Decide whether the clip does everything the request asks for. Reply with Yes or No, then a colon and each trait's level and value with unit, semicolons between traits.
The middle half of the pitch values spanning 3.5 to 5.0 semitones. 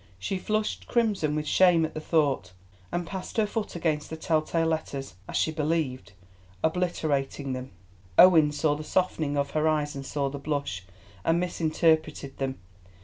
No: average, 3.0 semitones